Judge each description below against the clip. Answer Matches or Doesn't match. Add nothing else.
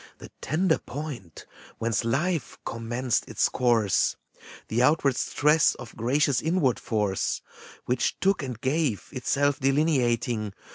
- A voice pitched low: Matches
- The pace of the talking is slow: Matches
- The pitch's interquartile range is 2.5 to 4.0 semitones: Doesn't match